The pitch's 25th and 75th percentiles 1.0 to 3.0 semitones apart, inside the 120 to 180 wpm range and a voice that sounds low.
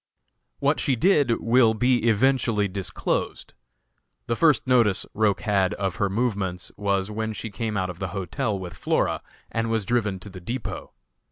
No: average, 3.4 semitones; average, 165 wpm; low, 105 Hz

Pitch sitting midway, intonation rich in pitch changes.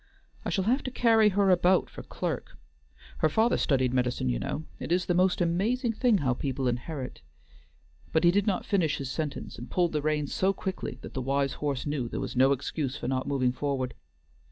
Yes: medium, 155 Hz; wide, 6.1 semitones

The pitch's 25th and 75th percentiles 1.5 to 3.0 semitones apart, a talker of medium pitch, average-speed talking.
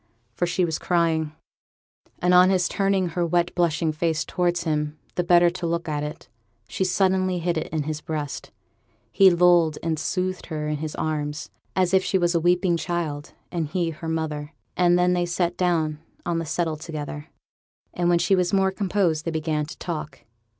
Yes: narrow, 2.4 semitones; medium, 170 Hz; average, 190 wpm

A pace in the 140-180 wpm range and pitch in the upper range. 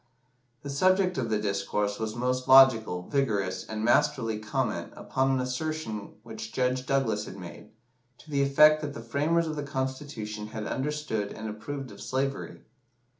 No: average, 160 wpm; low, 125 Hz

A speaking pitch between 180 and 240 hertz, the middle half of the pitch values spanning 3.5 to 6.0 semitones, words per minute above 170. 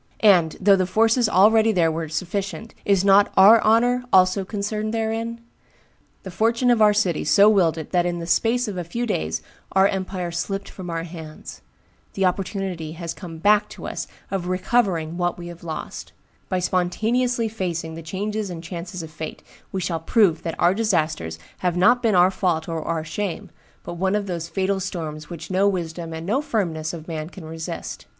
Yes: medium, 185 Hz; average, 3.9 semitones; average, 190 wpm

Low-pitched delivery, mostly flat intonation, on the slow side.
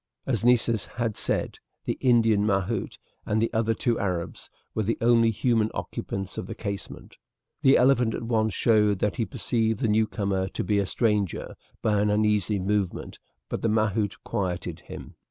No: low, 110 Hz; narrow, 2.3 semitones; average, 170 wpm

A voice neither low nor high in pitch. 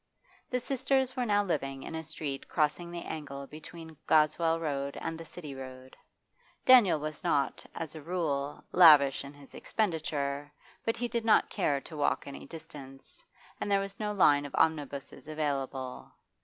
Yes: medium, 155 Hz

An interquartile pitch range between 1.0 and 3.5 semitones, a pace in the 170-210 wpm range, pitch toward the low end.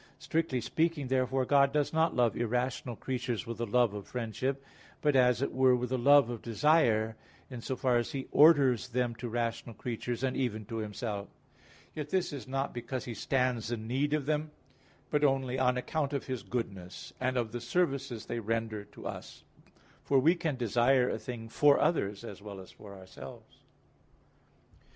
Yes: average, 3.1 semitones; average, 185 wpm; low, 125 Hz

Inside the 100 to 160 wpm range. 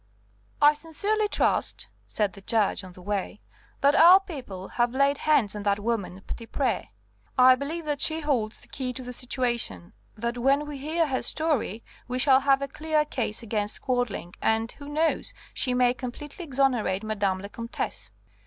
No: average, 170 wpm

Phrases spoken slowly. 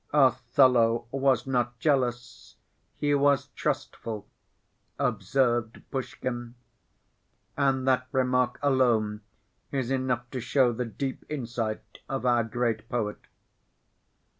Yes: slow, 100 wpm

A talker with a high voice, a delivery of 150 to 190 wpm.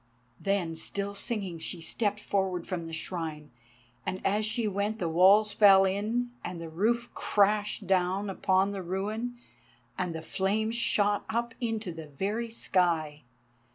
Yes: high, 195 Hz; average, 155 wpm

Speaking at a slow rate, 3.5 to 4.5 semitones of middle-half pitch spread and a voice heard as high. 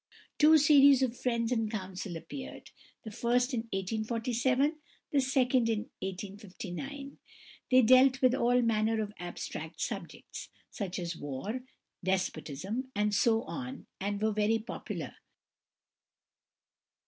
Yes: slow, 120 wpm; average, 4.0 semitones; high, 230 Hz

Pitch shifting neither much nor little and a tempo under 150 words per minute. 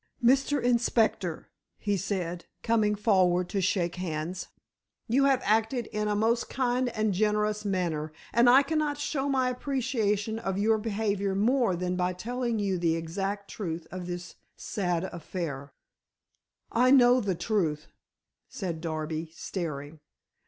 Yes: average, 5.0 semitones; average, 140 wpm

